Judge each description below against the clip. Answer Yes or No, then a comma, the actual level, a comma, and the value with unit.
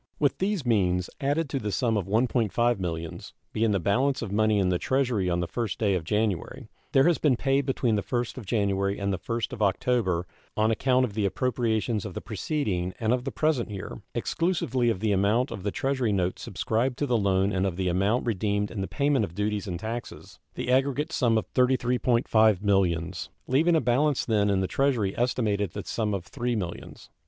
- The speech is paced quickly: Yes, fast, 210 wpm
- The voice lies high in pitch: No, low, 110 Hz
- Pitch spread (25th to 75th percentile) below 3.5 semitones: No, average, 4.4 semitones